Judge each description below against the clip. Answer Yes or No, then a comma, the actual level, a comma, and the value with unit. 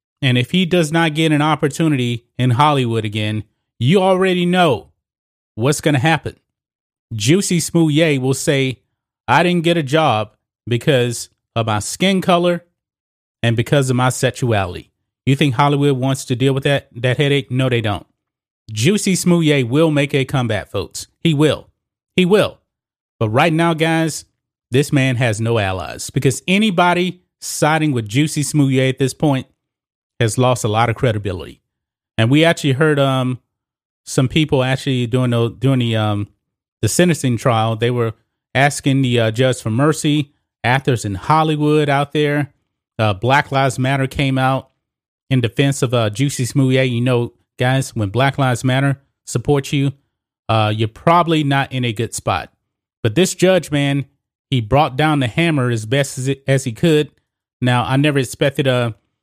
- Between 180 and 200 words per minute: No, average, 165 wpm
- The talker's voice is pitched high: No, low, 135 Hz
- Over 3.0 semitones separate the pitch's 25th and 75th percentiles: Yes, average, 4.1 semitones